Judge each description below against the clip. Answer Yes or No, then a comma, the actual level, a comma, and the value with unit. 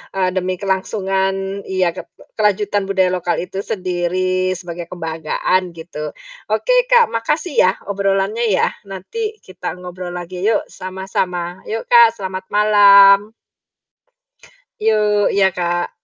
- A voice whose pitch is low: No, high, 190 Hz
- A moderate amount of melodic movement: No, narrow, 2.3 semitones